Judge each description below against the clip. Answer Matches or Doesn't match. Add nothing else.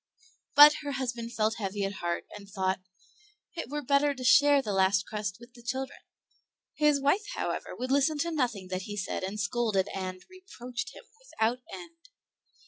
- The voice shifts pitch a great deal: Matches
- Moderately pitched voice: Doesn't match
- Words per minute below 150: Doesn't match